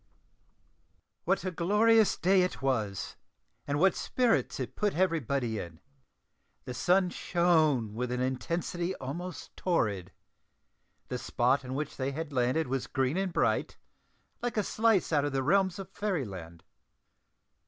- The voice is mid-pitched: Yes, medium, 155 Hz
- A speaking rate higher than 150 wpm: No, average, 145 wpm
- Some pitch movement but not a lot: No, wide, 6.6 semitones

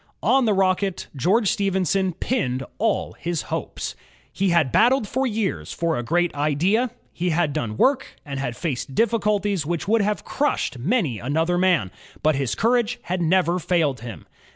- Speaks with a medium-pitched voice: Yes, medium, 180 Hz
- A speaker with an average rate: Yes, average, 170 wpm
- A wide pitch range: Yes, wide, 5.9 semitones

